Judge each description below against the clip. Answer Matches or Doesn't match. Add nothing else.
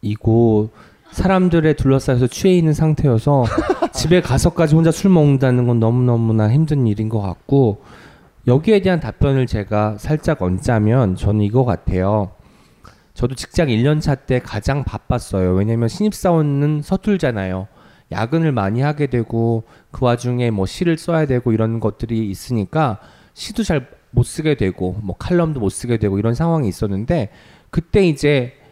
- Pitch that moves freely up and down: Matches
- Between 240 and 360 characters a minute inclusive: Matches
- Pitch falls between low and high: Doesn't match